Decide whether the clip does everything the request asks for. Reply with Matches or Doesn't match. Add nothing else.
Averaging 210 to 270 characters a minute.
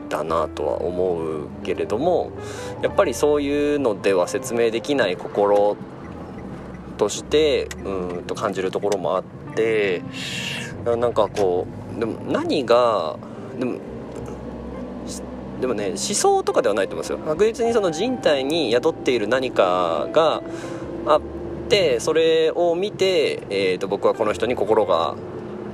Matches